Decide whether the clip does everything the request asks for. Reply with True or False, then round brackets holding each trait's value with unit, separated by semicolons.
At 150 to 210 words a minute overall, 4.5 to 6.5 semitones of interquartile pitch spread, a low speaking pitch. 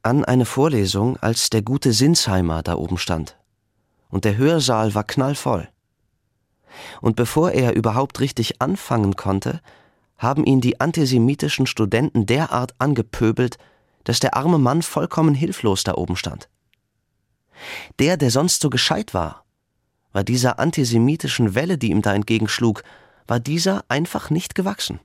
False (135 wpm; 4.8 semitones; 125 Hz)